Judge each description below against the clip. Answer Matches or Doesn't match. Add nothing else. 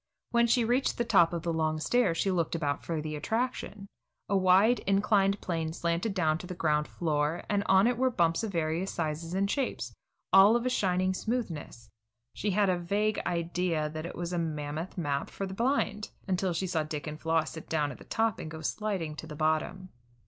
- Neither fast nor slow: Doesn't match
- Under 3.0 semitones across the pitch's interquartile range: Doesn't match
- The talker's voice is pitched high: Doesn't match